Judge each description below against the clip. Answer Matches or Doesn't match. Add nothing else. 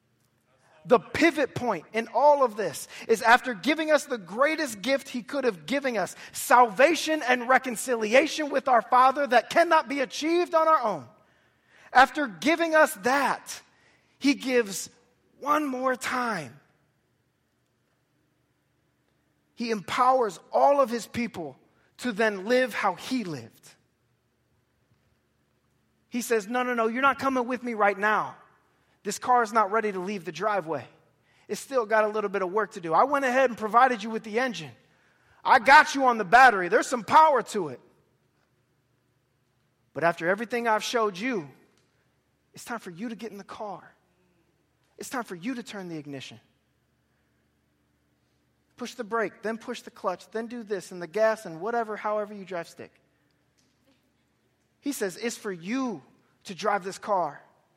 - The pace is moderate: Matches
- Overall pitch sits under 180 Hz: Doesn't match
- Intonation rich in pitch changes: Matches